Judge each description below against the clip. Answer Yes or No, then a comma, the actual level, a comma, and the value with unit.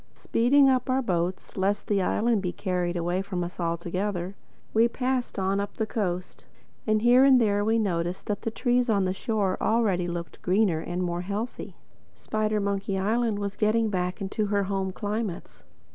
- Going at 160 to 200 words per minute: Yes, average, 175 wpm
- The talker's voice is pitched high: Yes, high, 200 Hz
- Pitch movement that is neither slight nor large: Yes, average, 3.5 semitones